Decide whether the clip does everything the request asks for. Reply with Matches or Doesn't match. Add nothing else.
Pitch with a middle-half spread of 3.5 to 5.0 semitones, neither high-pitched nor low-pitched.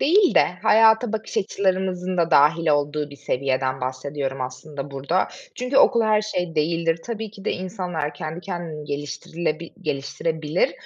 Matches